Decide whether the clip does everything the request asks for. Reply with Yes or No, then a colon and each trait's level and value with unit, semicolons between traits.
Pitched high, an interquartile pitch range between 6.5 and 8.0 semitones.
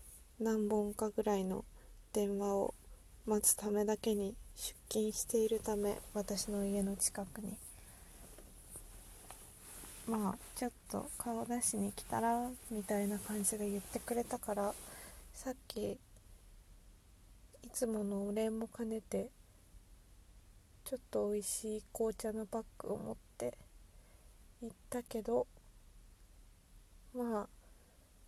Yes: high, 210 Hz; wide, 7.5 semitones